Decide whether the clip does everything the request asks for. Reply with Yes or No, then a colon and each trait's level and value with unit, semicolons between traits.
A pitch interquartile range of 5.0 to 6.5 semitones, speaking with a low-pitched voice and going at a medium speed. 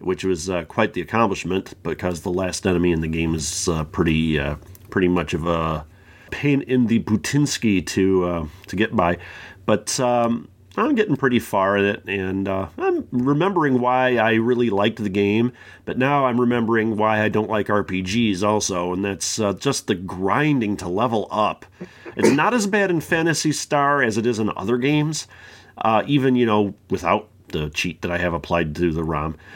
Yes: wide, 5.4 semitones; low, 105 Hz; average, 190 wpm